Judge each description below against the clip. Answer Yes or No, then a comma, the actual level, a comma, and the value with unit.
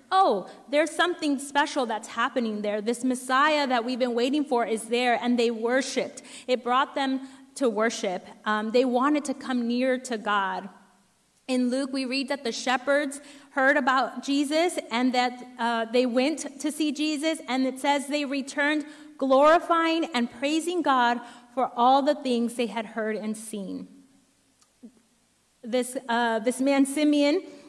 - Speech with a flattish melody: No, average, 3.1 semitones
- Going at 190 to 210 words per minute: No, average, 160 wpm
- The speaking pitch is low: No, very high, 260 Hz